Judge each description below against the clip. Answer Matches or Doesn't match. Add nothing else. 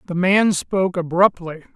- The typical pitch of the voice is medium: Matches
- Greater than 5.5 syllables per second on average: Doesn't match